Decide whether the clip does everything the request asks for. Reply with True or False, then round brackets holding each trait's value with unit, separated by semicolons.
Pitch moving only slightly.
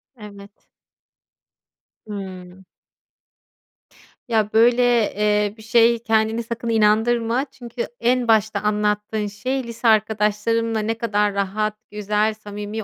True (1.7 semitones)